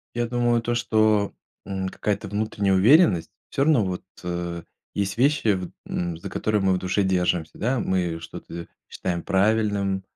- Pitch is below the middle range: Yes, low, 100 Hz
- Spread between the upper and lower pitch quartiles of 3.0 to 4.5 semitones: Yes, average, 3.5 semitones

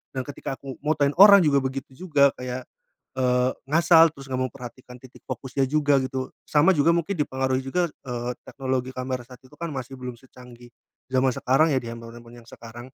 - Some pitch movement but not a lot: No, narrow, 2.3 semitones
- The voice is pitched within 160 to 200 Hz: No, low, 130 Hz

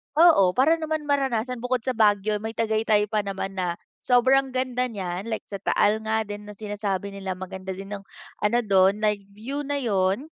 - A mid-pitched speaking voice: No, high, 215 Hz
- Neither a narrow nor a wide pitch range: Yes, average, 4.2 semitones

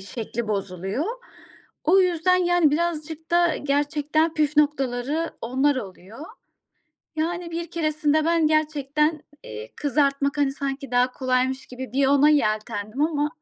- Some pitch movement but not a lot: Yes, average, 3.4 semitones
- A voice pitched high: Yes, very high, 290 Hz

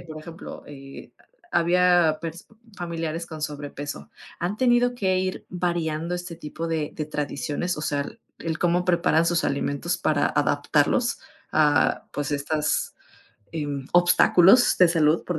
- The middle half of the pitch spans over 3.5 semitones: No, average, 2.8 semitones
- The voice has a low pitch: No, medium, 165 Hz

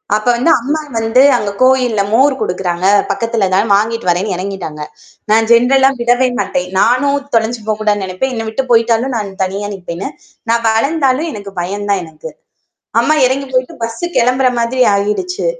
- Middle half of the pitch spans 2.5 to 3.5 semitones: No, average, 4.3 semitones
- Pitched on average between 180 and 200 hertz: No, high, 225 Hz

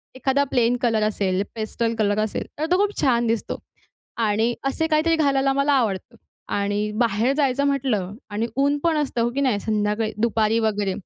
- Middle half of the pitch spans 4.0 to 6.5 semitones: Yes, average, 4.5 semitones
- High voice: Yes, high, 235 Hz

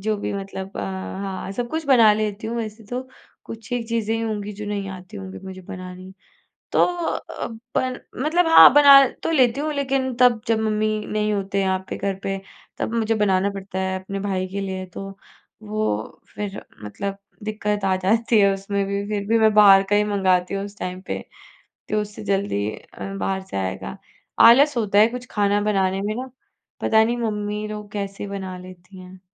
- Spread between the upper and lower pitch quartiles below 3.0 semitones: Yes, narrow, 2.5 semitones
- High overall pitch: Yes, high, 205 Hz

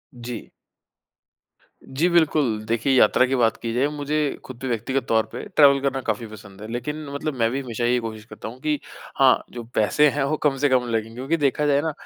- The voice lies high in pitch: No, low, 130 Hz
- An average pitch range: Yes, average, 3.8 semitones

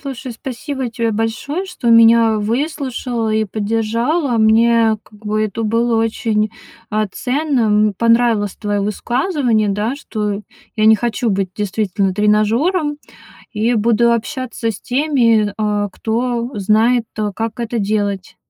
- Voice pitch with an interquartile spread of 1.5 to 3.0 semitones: Yes, narrow, 2.4 semitones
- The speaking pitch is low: No, high, 225 Hz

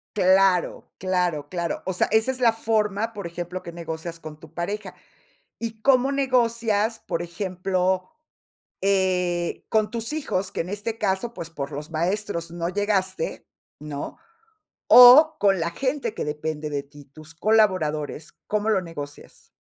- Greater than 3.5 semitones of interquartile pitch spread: Yes, average, 4.6 semitones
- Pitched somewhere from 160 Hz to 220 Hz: Yes, medium, 185 Hz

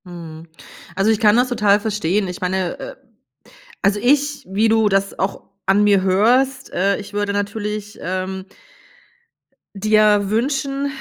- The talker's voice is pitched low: No, high, 205 Hz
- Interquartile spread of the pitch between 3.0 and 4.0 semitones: No, narrow, 2.6 semitones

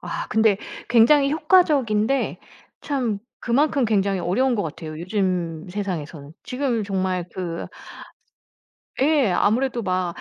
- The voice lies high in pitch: Yes, high, 210 Hz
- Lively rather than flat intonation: Yes, wide, 6.2 semitones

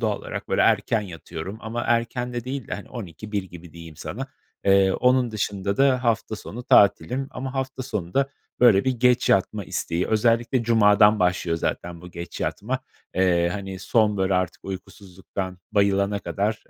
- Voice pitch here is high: No, low, 105 Hz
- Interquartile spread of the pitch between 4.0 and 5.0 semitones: Yes, average, 4.3 semitones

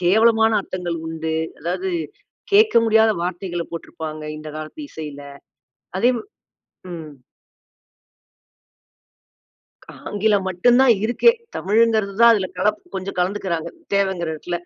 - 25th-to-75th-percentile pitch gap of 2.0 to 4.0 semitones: No, average, 4.5 semitones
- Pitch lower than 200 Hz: Yes, high, 190 Hz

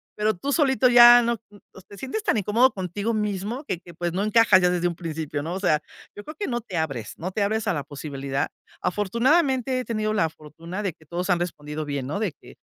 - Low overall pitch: No, high, 190 Hz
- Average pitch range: No, wide, 5.9 semitones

